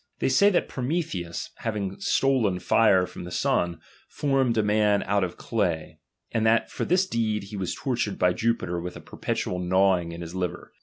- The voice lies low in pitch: Yes, low, 100 Hz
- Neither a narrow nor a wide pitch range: Yes, average, 4.4 semitones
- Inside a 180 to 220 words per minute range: Yes, average, 200 wpm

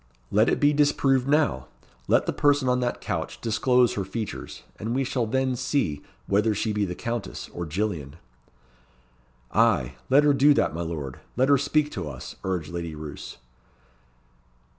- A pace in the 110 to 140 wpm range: No, average, 165 wpm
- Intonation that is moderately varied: No, wide, 7.6 semitones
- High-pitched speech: No, low, 115 Hz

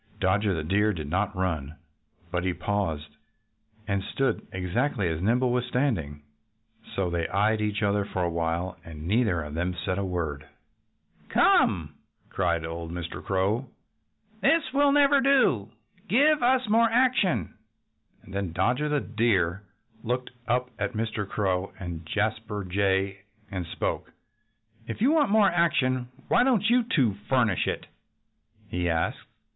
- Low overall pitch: Yes, low, 100 Hz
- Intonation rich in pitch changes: Yes, wide, 6.5 semitones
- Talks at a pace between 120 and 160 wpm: Yes, average, 145 wpm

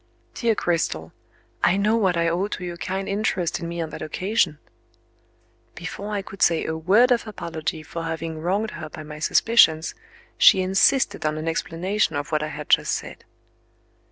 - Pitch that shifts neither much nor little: Yes, average, 3.8 semitones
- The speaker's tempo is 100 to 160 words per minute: No, average, 180 wpm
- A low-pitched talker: No, medium, 175 Hz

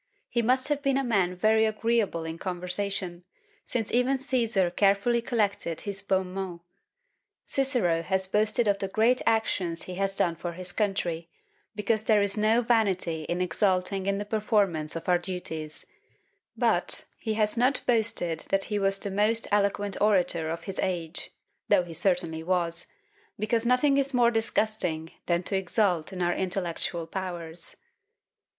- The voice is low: No, high, 195 Hz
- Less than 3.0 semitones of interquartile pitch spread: No, average, 3.9 semitones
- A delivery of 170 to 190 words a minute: No, average, 155 wpm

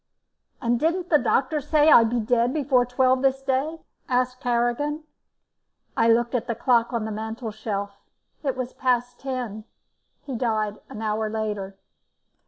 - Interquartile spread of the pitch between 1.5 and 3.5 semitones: Yes, average, 3.0 semitones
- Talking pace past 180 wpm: No, average, 150 wpm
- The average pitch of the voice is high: Yes, high, 245 Hz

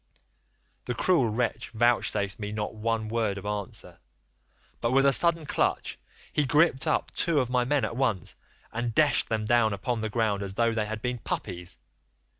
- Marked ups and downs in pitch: No, average, 3.1 semitones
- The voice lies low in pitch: Yes, low, 115 Hz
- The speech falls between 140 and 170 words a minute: No, average, 180 wpm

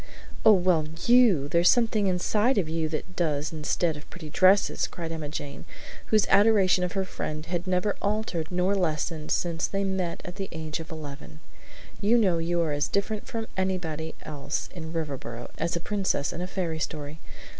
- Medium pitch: Yes, medium, 175 Hz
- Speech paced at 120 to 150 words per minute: No, average, 180 wpm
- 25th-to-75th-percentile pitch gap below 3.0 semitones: No, average, 3.6 semitones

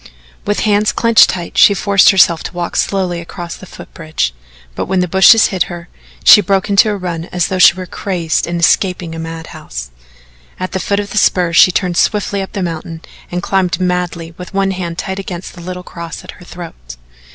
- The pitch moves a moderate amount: No, narrow, 2.3 semitones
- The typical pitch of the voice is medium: Yes, medium, 180 Hz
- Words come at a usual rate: No, fast, 210 wpm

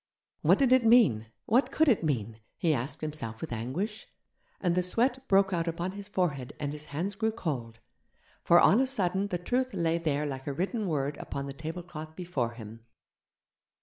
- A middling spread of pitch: No, wide, 6.3 semitones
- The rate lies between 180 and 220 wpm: Yes, average, 185 wpm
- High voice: No, medium, 170 Hz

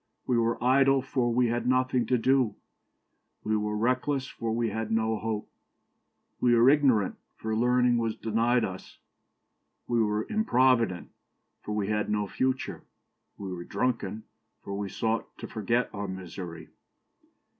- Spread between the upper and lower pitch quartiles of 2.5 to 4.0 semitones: Yes, average, 3.0 semitones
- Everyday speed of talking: Yes, average, 145 wpm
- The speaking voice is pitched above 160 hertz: No, low, 115 Hz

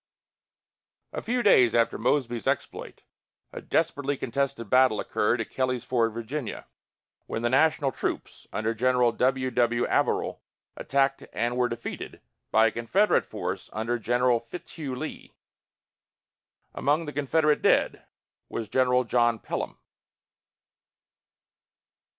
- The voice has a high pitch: No, low, 125 Hz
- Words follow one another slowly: Yes, slow, 120 wpm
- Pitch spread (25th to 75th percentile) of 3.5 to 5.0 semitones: No, average, 3.0 semitones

